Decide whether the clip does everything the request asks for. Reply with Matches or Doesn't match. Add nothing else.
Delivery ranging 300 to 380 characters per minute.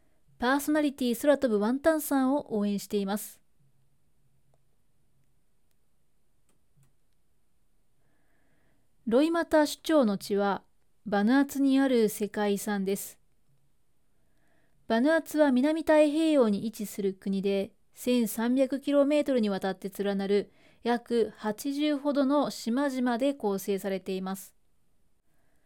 Doesn't match